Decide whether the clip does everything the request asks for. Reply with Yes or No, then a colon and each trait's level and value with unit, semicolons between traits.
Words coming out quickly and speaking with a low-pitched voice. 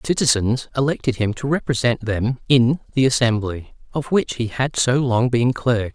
No: average, 180 wpm; low, 125 Hz